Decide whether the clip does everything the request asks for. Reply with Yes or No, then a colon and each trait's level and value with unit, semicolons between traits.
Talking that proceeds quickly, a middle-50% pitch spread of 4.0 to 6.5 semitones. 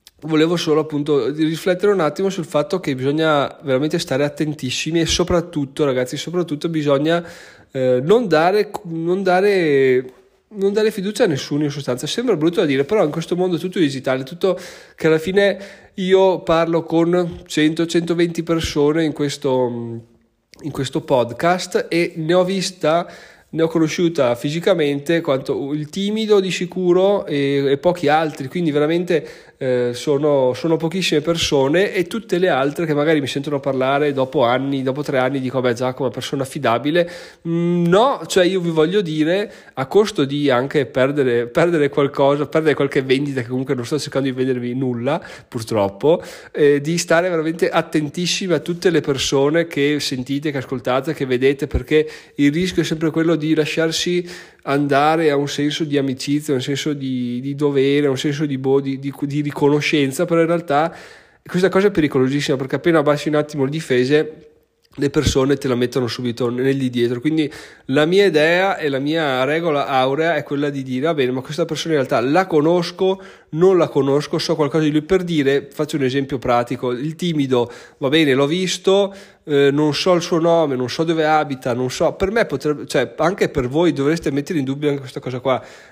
No: fast, 180 wpm; average, 3.6 semitones